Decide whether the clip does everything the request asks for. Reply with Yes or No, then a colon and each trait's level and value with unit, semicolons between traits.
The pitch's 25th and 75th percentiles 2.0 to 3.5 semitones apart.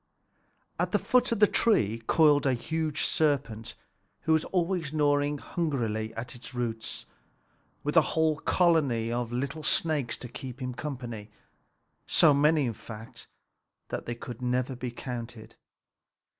No: average, 4.7 semitones